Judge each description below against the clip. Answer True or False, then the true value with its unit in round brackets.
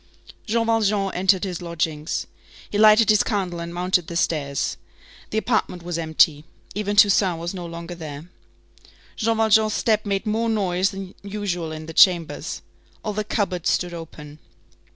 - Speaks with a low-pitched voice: False (185 Hz)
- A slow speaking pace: False (155 wpm)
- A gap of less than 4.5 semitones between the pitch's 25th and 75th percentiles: True (3.8 semitones)